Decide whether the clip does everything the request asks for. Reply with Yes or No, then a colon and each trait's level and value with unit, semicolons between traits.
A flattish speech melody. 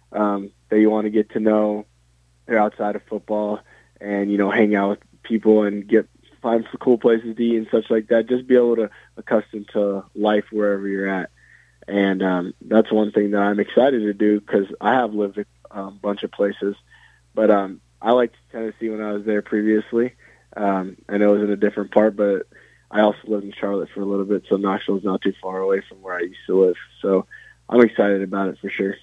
Yes: narrow, 1.6 semitones